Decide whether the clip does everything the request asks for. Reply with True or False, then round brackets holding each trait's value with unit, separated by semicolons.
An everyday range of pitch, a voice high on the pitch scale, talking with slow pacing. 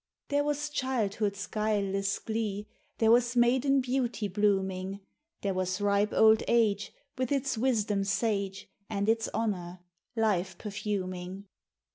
True (3.1 semitones; 210 Hz; 120 wpm)